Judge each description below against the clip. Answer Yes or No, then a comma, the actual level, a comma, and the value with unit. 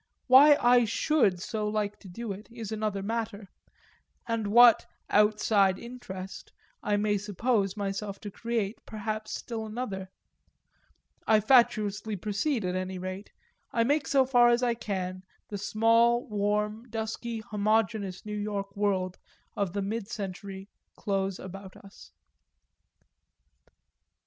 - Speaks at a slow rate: Yes, slow, 130 wpm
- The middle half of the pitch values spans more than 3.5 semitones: No, narrow, 2.6 semitones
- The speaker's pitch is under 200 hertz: No, high, 210 Hz